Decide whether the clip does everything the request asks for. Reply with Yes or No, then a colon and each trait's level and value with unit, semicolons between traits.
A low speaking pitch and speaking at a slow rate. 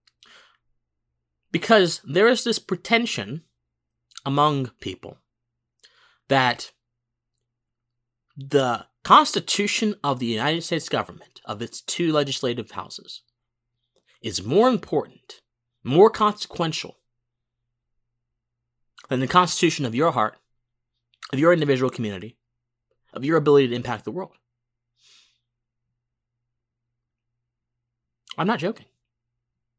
Yes: low, 120 Hz; slow, 90 wpm